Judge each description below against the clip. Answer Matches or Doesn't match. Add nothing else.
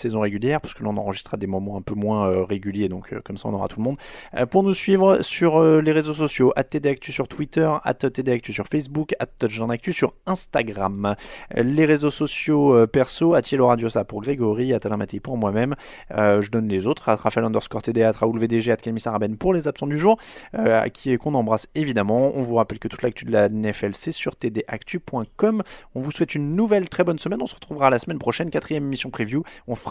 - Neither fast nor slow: Doesn't match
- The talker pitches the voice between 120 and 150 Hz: Matches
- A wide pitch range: Matches